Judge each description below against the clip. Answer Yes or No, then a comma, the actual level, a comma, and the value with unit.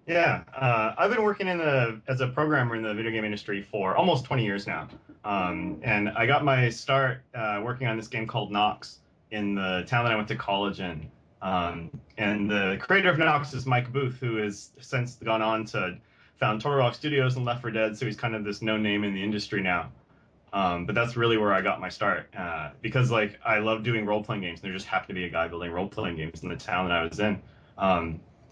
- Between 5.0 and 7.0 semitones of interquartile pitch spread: No, average, 4.0 semitones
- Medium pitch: No, low, 110 Hz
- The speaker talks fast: Yes, fast, 240 wpm